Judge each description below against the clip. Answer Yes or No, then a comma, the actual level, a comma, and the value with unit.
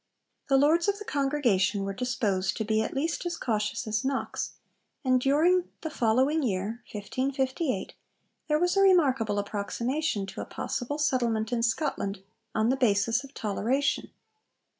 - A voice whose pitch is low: No, very high, 255 Hz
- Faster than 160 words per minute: No, average, 150 wpm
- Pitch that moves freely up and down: No, average, 5.0 semitones